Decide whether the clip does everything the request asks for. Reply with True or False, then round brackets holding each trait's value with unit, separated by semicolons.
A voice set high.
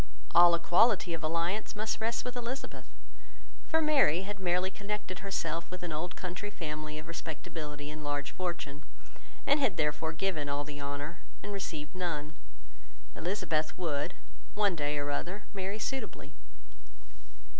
False (170 Hz)